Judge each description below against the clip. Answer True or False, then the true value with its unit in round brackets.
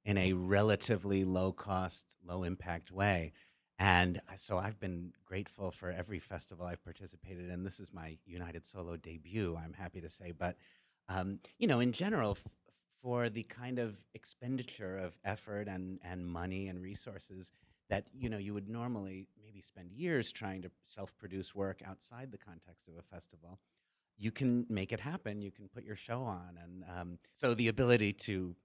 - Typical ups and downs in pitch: True (3.0 semitones)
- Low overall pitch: True (95 Hz)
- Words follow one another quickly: False (180 wpm)